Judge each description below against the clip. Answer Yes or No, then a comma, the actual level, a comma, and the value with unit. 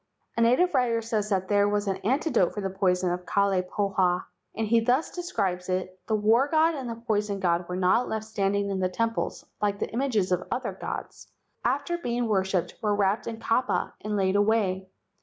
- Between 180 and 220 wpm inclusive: Yes, average, 200 wpm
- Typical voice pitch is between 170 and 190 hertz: No, high, 205 Hz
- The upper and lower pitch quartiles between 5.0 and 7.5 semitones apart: No, average, 3.5 semitones